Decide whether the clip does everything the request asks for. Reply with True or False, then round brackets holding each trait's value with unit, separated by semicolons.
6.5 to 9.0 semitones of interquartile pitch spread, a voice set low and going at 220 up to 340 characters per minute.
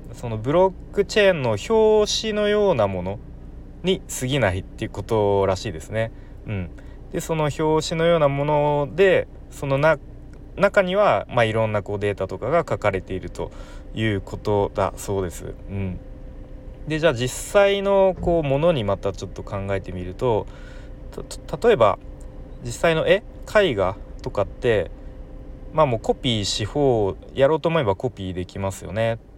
True (8.4 semitones; 115 Hz; 310 characters per minute)